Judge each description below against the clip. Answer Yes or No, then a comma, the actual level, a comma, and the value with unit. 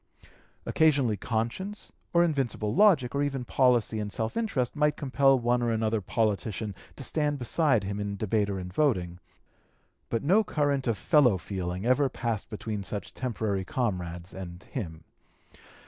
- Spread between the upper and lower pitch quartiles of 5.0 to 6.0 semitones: Yes, wide, 5.5 semitones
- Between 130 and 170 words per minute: Yes, average, 150 wpm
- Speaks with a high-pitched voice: No, low, 115 Hz